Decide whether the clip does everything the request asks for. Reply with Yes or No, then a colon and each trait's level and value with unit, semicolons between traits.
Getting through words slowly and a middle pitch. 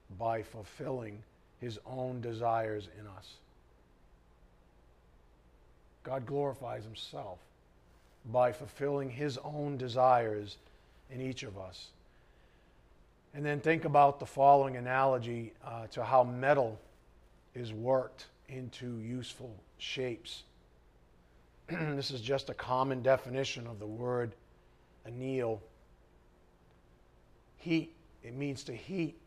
No: slow, 105 wpm; low, 115 Hz